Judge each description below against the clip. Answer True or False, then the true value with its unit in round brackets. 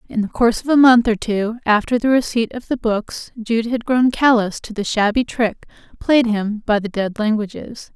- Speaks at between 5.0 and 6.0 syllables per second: False (4.8 syllables/s)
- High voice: True (225 Hz)